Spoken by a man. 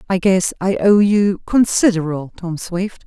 No: female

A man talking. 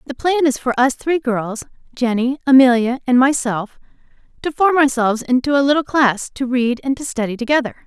No: female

